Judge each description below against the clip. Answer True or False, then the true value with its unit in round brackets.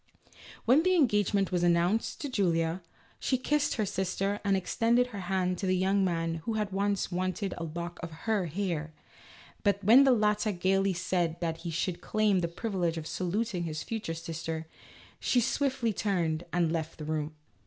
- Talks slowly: False (175 wpm)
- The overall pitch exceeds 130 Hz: True (185 Hz)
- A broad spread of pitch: False (3.8 semitones)